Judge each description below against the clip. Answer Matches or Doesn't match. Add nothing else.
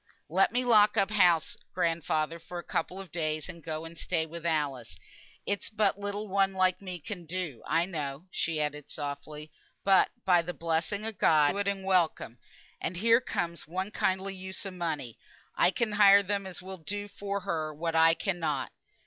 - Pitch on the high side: Doesn't match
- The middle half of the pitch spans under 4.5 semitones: Matches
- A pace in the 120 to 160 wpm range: Doesn't match